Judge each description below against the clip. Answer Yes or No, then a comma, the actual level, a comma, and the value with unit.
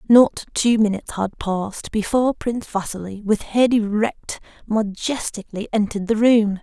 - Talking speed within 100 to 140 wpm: Yes, slow, 135 wpm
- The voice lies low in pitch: No, high, 215 Hz